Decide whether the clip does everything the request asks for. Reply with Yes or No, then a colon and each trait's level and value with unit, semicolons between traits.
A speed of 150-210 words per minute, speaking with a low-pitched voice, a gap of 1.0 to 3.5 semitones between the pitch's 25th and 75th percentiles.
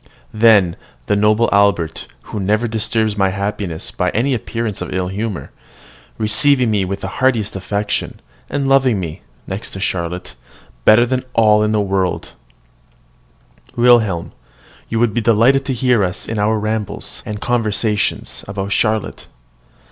No: average, 140 wpm; low, 105 Hz; average, 2.9 semitones